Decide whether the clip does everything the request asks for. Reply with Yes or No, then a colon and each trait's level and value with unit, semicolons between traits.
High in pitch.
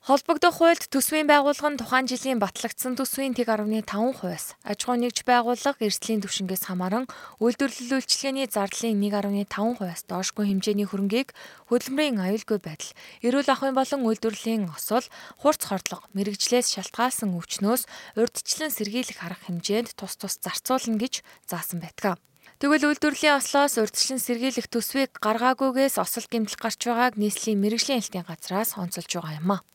Yes: high, 230 Hz